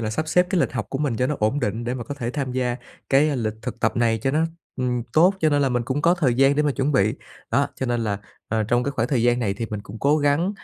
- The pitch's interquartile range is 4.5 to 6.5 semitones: No, average, 3.7 semitones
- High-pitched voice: No, low, 130 Hz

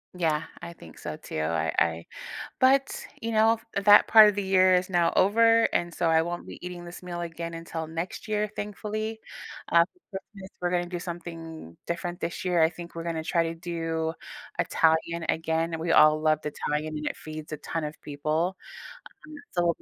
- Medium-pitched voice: Yes, medium, 170 Hz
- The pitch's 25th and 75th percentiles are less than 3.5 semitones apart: Yes, narrow, 2.5 semitones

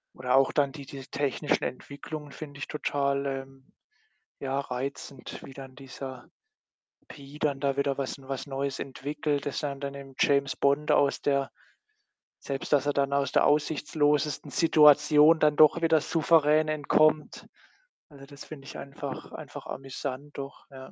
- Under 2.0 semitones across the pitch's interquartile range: Yes, narrow, 1.5 semitones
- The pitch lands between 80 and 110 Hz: No, medium, 140 Hz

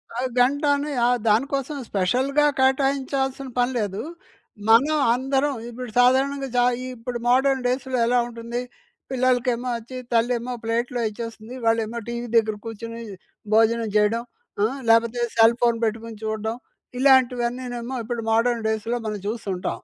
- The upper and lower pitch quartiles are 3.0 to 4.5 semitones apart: No, narrow, 2.4 semitones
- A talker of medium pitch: No, high, 240 Hz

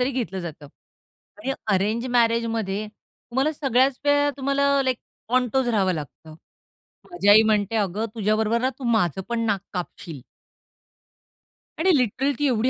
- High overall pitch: Yes, high, 230 Hz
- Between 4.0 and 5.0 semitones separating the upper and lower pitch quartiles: Yes, average, 4.5 semitones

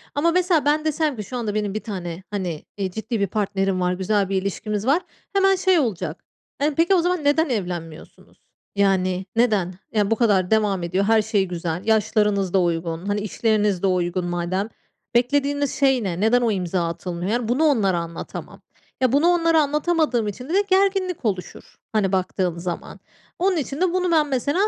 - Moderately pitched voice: No, high, 215 Hz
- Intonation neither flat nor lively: No, wide, 7.5 semitones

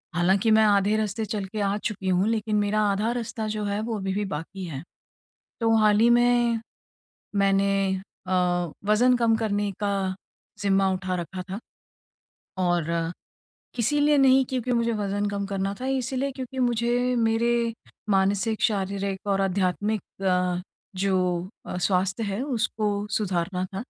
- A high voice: Yes, high, 205 Hz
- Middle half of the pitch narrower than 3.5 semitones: Yes, average, 3.0 semitones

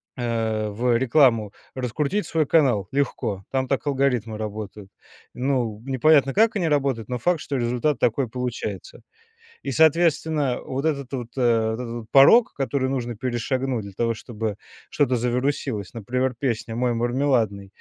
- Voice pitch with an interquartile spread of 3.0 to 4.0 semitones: Yes, average, 3.4 semitones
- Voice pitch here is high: No, low, 125 Hz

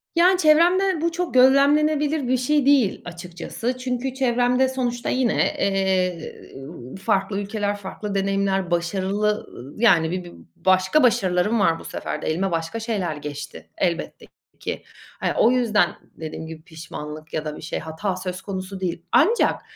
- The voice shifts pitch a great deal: Yes, wide, 6.6 semitones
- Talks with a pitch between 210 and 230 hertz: No, high, 195 Hz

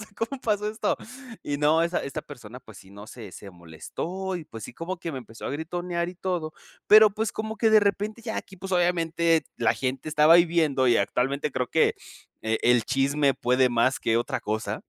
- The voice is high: No, medium, 155 Hz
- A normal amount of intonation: No, wide, 6.7 semitones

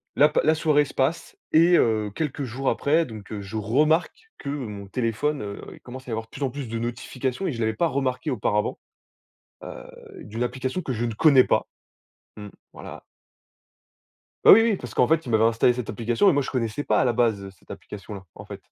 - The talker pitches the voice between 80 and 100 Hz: No, low, 125 Hz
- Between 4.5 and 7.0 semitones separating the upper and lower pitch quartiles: Yes, average, 4.8 semitones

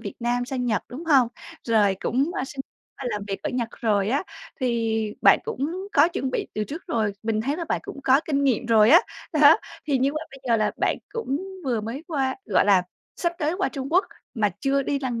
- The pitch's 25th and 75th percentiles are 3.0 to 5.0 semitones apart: Yes, average, 4.6 semitones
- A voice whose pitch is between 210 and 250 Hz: No, very high, 260 Hz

